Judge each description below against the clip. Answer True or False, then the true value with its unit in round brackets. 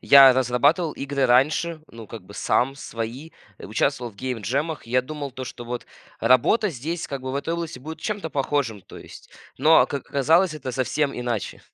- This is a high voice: False (135 Hz)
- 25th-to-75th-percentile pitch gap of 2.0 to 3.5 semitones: False (3.9 semitones)